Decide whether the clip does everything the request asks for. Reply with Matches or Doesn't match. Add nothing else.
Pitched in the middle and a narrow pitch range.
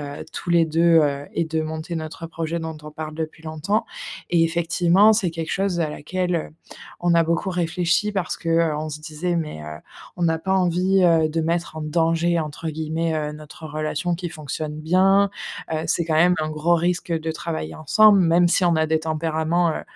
Matches